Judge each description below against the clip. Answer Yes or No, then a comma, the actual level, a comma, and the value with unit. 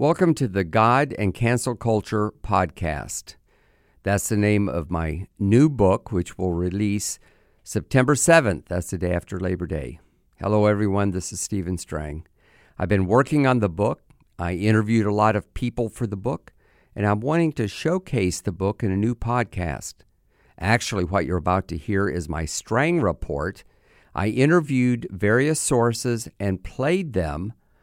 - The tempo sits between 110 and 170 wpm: Yes, average, 160 wpm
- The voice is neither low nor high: No, low, 105 Hz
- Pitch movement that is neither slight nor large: Yes, average, 4.8 semitones